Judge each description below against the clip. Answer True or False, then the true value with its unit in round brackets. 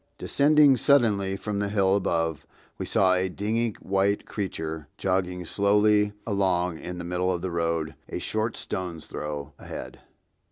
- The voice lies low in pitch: True (95 Hz)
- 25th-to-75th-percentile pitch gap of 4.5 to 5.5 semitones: False (3.1 semitones)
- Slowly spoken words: False (150 wpm)